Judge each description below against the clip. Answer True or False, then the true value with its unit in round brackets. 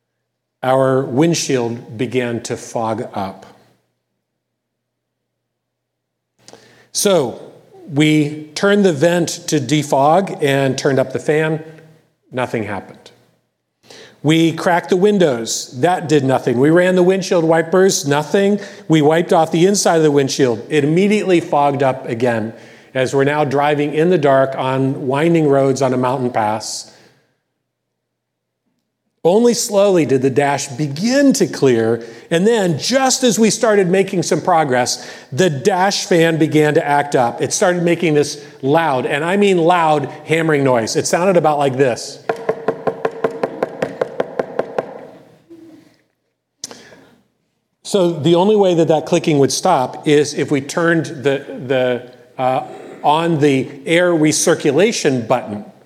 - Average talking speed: False (130 wpm)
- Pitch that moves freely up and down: False (4.9 semitones)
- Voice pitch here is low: False (150 Hz)